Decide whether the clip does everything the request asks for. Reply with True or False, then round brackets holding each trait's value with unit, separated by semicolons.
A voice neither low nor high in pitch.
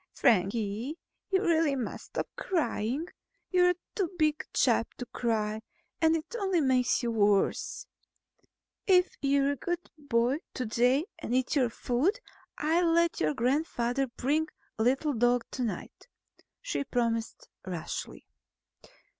False (265 Hz)